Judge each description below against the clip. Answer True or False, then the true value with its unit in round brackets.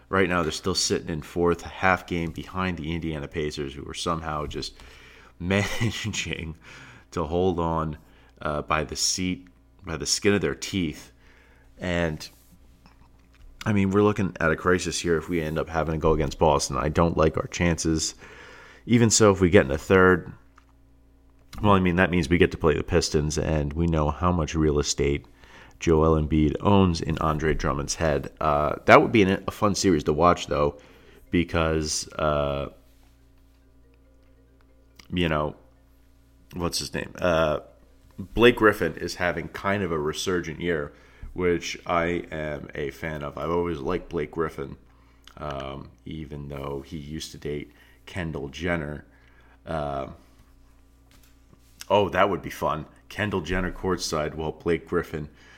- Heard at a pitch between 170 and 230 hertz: False (80 Hz)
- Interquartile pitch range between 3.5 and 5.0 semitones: True (4.1 semitones)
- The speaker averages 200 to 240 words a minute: False (160 wpm)